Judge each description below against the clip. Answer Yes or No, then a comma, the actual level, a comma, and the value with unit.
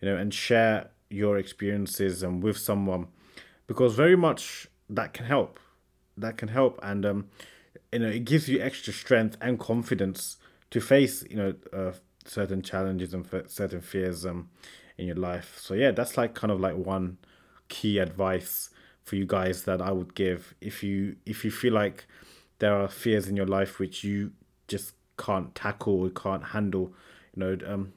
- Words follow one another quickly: No, average, 180 wpm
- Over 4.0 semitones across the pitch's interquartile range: No, narrow, 2.6 semitones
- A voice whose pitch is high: No, low, 100 Hz